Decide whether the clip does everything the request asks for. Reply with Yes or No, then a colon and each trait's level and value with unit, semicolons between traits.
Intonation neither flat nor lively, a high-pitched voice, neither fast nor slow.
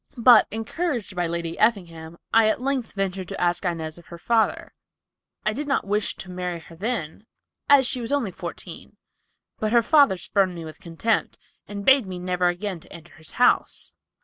Yes: average, 5.0 semitones; high, 195 Hz; average, 180 wpm